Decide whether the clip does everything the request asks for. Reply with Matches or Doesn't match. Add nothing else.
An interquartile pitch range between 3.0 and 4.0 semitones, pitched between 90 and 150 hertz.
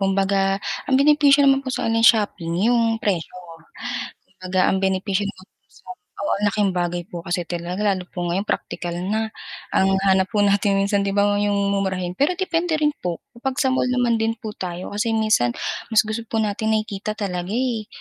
Doesn't match